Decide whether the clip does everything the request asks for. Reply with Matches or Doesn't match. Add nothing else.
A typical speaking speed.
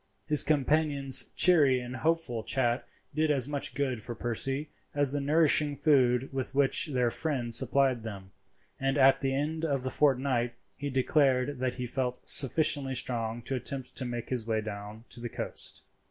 Matches